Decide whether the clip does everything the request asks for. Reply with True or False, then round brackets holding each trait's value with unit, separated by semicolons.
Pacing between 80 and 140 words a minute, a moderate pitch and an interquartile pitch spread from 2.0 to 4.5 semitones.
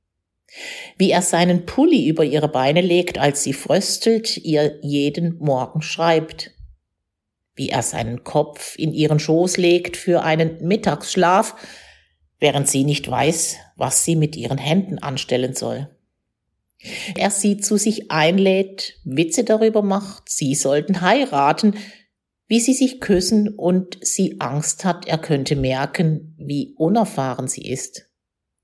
False (130 wpm; 160 Hz; 5.3 semitones)